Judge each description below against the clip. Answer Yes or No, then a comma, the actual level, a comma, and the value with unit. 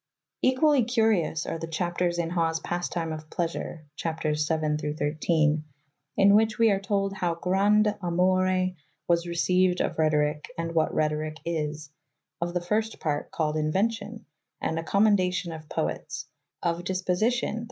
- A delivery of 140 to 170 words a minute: Yes, average, 150 wpm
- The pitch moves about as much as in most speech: Yes, average, 3.8 semitones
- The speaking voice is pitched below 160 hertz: No, medium, 175 Hz